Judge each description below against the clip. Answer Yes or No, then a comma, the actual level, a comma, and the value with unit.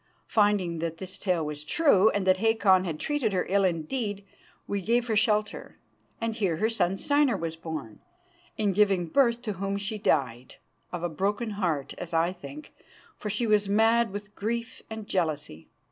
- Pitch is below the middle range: No, high, 200 Hz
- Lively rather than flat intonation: No, average, 4.3 semitones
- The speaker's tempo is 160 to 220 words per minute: Yes, average, 175 wpm